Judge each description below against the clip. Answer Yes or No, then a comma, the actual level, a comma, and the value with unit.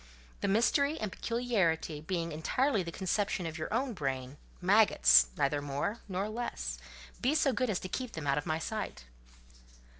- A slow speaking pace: No, average, 155 wpm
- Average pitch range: No, wide, 7.4 semitones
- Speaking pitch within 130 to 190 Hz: Yes, medium, 185 Hz